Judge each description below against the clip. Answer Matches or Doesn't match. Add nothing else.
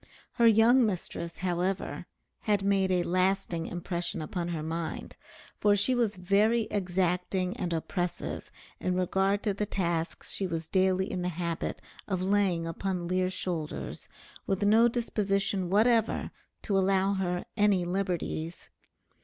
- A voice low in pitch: Doesn't match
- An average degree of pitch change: Doesn't match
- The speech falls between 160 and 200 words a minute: Doesn't match